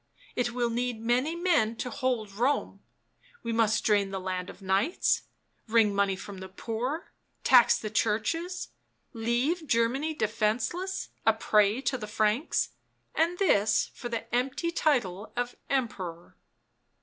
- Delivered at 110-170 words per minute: Yes, average, 140 wpm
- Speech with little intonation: No, average, 4.2 semitones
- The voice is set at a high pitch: Yes, high, 230 Hz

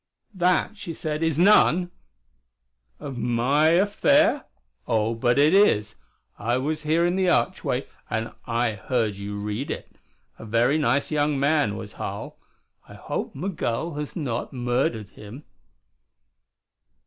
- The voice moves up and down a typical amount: No, wide, 6.3 semitones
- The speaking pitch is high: No, low, 135 Hz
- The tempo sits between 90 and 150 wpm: Yes, slow, 135 wpm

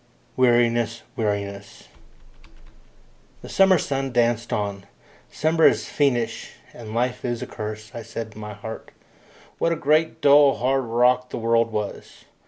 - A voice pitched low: Yes, low, 120 Hz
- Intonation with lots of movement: No, average, 3.5 semitones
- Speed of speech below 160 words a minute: Yes, average, 140 wpm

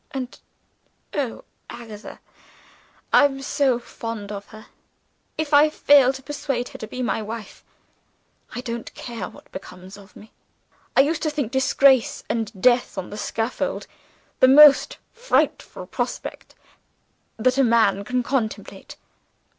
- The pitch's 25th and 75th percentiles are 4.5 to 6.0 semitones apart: No, average, 3.8 semitones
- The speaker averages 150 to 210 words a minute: No, average, 140 wpm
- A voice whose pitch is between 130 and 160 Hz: No, high, 245 Hz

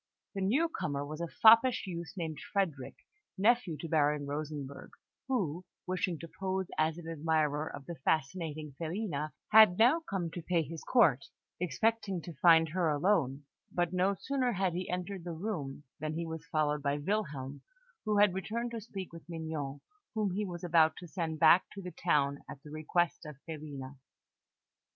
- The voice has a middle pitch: Yes, medium, 165 Hz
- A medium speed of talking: Yes, average, 170 wpm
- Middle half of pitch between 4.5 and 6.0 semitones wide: No, average, 4.1 semitones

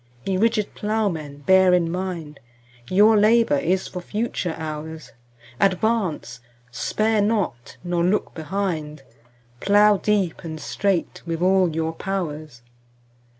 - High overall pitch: No, medium, 180 Hz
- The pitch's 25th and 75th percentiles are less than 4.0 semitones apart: No, average, 4.6 semitones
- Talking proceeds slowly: Yes, slow, 110 wpm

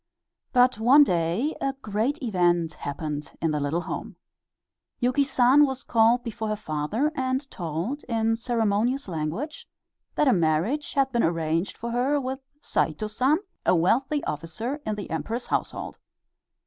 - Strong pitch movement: Yes, wide, 7.7 semitones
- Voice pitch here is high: Yes, high, 225 Hz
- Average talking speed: Yes, average, 150 wpm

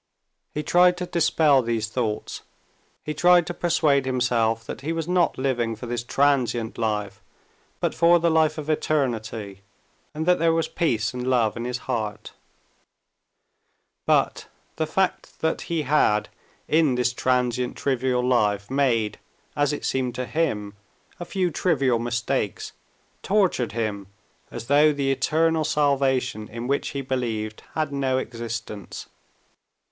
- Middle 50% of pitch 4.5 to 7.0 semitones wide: Yes, average, 5.0 semitones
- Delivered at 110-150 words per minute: Yes, average, 140 wpm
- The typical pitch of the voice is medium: No, low, 130 Hz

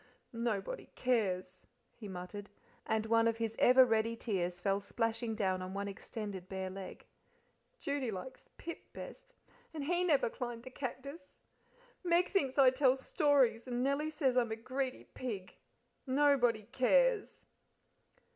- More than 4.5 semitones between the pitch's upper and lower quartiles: Yes, average, 5.2 semitones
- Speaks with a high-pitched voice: Yes, high, 240 Hz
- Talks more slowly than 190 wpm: Yes, average, 140 wpm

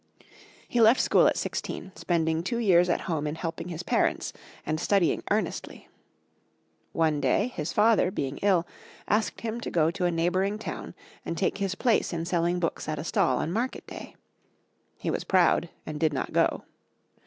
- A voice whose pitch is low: No, medium, 175 Hz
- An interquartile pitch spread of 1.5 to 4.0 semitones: Yes, average, 3.6 semitones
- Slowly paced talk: No, average, 175 wpm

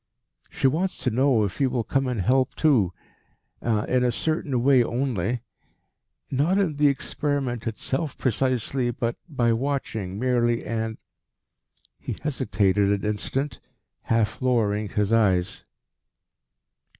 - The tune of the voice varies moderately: Yes, average, 3.7 semitones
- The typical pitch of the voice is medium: No, low, 120 Hz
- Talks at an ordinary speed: No, slow, 125 wpm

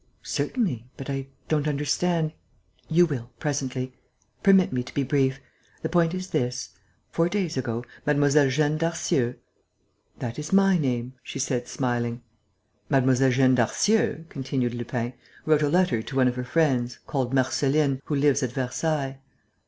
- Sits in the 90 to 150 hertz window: Yes, low, 135 Hz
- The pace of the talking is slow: No, average, 150 wpm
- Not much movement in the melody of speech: No, average, 3.7 semitones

